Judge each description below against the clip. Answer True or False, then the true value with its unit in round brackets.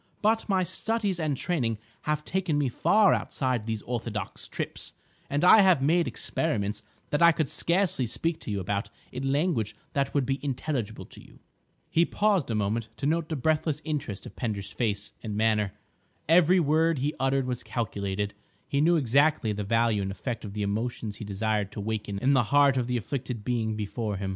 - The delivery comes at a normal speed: True (190 wpm)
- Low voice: True (130 Hz)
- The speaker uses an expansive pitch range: True (6.5 semitones)